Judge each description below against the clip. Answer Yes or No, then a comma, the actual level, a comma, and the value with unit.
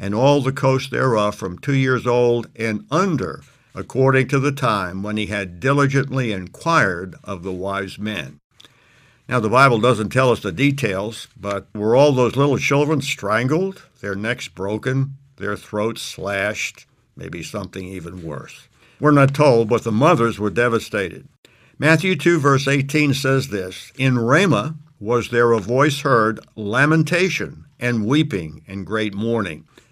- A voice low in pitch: Yes, low, 120 Hz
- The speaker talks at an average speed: Yes, average, 150 wpm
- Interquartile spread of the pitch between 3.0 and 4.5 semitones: No, average, 5.1 semitones